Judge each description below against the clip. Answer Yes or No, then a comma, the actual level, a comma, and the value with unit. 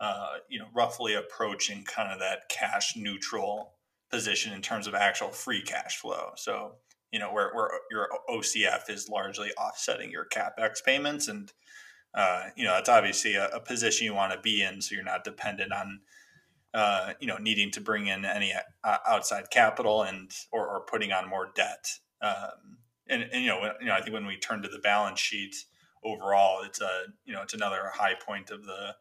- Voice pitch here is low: Yes, low, 105 Hz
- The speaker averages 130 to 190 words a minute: No, average, 200 wpm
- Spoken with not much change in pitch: Yes, narrow, 2.3 semitones